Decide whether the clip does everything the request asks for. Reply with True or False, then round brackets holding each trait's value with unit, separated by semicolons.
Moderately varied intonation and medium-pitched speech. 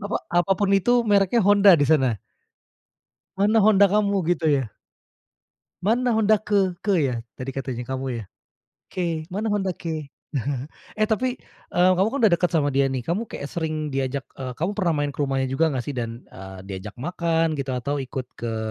False (6.9 semitones; 165 Hz)